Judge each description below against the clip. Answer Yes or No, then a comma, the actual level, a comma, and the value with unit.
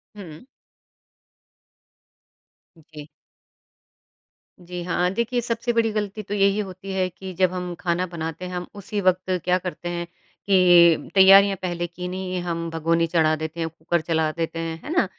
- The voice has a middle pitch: Yes, medium, 180 Hz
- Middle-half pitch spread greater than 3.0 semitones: No, narrow, 2.5 semitones